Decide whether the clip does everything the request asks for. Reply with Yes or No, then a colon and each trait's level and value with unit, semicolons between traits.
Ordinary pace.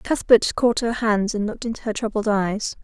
No: fast, 210 wpm